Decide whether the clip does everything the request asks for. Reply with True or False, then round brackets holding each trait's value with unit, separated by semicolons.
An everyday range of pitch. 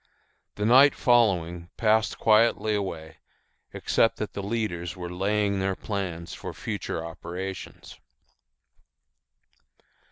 True (3.7 semitones)